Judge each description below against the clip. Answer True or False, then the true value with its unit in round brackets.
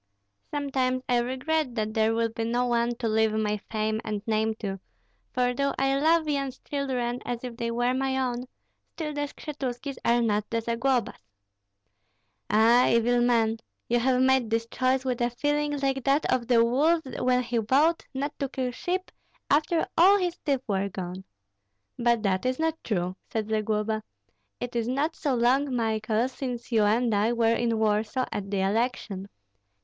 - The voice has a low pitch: False (240 Hz)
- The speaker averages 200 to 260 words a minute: False (175 wpm)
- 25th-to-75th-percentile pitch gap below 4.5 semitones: True (3.3 semitones)